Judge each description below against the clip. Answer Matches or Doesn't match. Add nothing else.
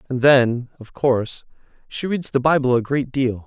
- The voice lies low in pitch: Matches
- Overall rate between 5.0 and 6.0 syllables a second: Doesn't match